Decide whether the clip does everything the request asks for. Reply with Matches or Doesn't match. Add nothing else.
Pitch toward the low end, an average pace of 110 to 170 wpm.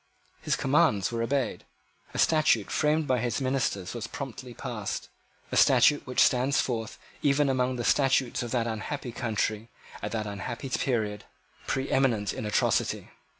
Matches